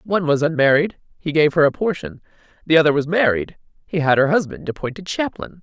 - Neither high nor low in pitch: Yes, medium, 165 Hz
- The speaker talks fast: No, average, 170 wpm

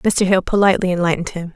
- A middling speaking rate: Yes, average, 195 wpm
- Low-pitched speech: No, medium, 185 Hz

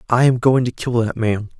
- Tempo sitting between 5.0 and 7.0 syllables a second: Yes, 5.2 syllables/s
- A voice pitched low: Yes, low, 120 Hz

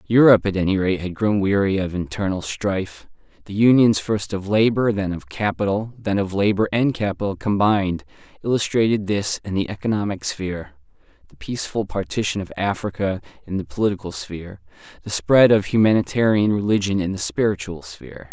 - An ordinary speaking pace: Yes, average, 155 wpm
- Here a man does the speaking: Yes, male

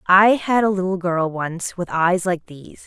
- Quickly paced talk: Yes, fast, 210 wpm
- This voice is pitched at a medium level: Yes, medium, 180 Hz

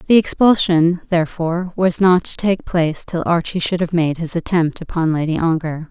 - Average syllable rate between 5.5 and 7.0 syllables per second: No, 5.2 syllables/s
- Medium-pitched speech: Yes, medium, 170 Hz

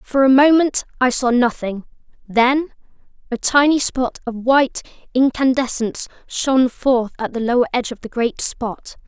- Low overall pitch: No, very high, 250 Hz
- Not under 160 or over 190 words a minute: No, average, 145 wpm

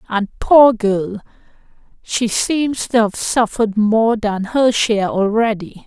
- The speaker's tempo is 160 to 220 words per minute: No, slow, 135 wpm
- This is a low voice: No, high, 215 Hz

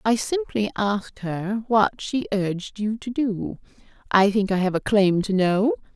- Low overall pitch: No, high, 205 Hz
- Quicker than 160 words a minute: Yes, average, 170 wpm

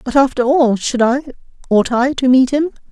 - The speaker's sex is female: Yes, female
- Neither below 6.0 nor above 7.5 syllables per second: No, 4.9 syllables/s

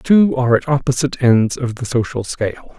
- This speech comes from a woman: No, male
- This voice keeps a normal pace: No, fast, 215 wpm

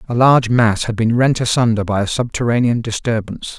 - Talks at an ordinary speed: Yes, average, 185 wpm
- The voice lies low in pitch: Yes, low, 115 Hz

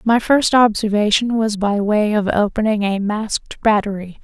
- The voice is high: Yes, high, 215 Hz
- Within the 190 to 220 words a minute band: No, average, 155 wpm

